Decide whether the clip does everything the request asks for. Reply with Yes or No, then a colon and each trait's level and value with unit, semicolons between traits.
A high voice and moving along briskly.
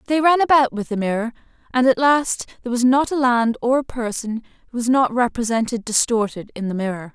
Yes: high, 240 Hz; fast, 210 wpm